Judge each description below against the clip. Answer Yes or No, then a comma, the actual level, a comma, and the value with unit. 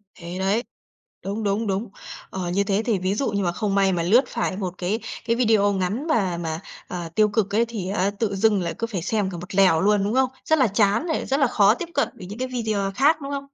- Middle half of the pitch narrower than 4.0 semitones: Yes, average, 3.5 semitones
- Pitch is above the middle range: Yes, high, 205 Hz